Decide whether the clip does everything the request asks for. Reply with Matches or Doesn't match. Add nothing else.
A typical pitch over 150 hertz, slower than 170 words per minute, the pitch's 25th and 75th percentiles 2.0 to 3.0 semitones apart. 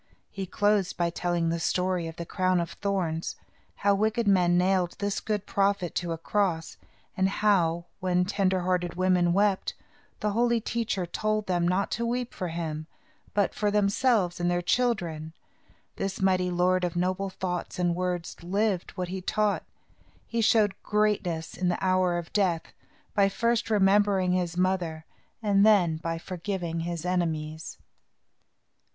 Matches